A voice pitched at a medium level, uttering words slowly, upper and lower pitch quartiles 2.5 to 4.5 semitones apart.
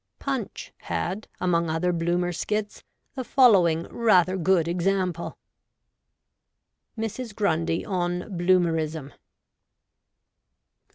Yes: medium, 180 Hz; slow, 90 wpm; average, 2.8 semitones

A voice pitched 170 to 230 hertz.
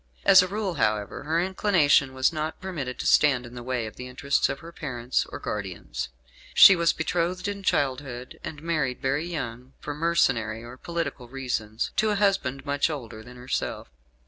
No: medium, 140 Hz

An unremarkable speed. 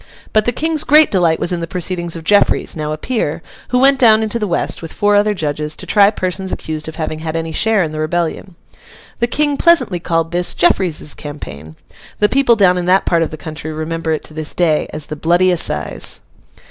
No: fast, 220 wpm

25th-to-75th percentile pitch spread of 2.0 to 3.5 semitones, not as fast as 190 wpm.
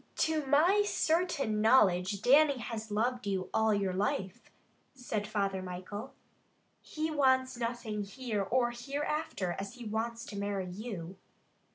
No: average, 4.6 semitones; slow, 135 wpm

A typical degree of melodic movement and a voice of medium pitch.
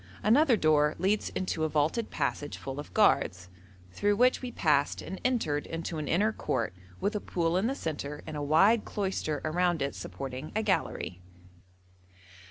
No: wide, 6.0 semitones; medium, 165 Hz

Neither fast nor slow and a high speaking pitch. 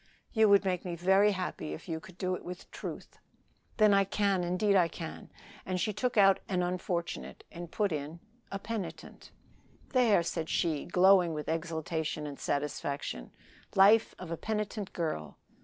No: average, 165 wpm; medium, 180 Hz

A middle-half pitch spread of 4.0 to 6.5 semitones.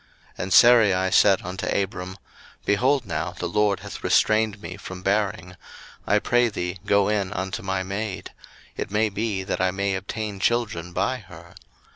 No: narrow, 2.4 semitones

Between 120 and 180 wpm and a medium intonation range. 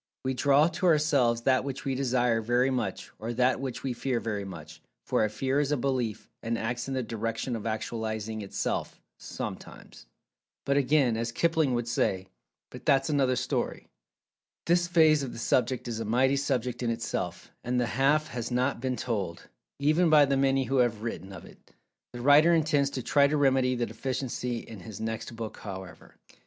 No: average, 190 wpm; average, 3.3 semitones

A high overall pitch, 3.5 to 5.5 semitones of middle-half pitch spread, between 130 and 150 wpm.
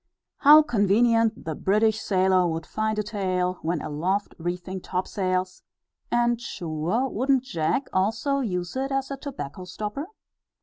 Yes: high, 200 Hz; average, 4.9 semitones; slow, 135 wpm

